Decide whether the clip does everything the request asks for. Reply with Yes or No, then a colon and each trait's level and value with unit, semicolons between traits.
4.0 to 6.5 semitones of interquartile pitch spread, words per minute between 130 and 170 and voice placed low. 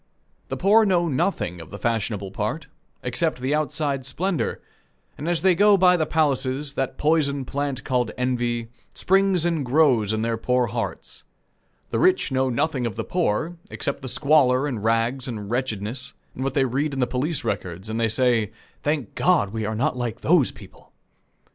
No: average, 5.1 semitones; average, 180 wpm; low, 130 Hz